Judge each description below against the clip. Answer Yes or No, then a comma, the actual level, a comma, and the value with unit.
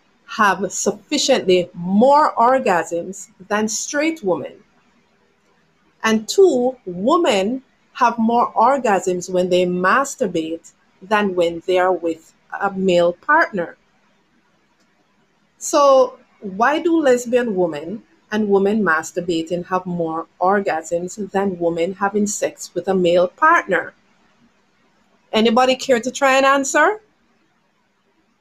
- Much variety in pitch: Yes, wide, 5.9 semitones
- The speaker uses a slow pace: Yes, slow, 105 wpm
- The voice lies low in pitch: No, high, 200 Hz